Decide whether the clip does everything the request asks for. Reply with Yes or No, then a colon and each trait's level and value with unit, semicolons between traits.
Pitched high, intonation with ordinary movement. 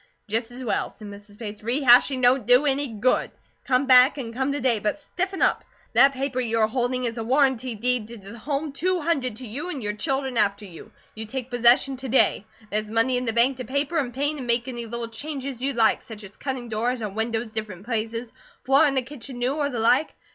Yes: high, 245 Hz; average, 3.1 semitones